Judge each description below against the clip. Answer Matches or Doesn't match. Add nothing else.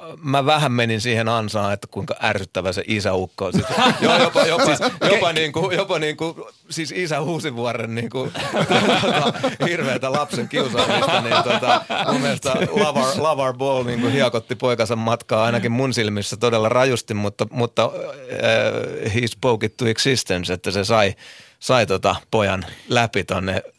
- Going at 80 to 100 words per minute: Doesn't match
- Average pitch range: Matches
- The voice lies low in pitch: Matches